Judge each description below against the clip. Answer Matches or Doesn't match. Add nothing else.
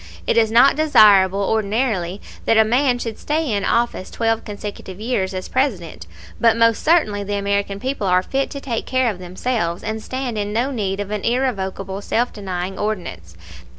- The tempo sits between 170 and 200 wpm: Matches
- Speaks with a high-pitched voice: Matches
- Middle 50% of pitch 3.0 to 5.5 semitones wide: Matches